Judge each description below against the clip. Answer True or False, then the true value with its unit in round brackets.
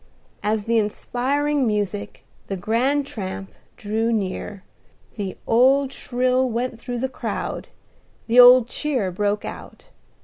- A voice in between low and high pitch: False (230 Hz)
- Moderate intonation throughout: True (3.7 semitones)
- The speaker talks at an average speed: False (125 wpm)